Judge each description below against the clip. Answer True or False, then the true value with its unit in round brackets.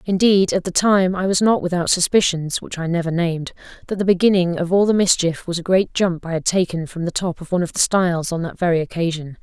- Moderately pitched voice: True (175 Hz)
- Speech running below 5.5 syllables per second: False (5.7 syllables/s)